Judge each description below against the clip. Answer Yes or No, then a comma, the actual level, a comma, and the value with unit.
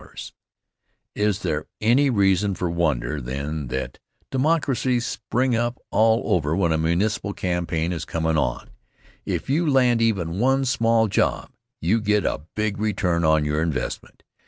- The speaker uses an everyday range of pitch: No, wide, 6.2 semitones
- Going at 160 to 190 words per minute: No, average, 150 wpm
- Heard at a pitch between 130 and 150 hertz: No, low, 100 Hz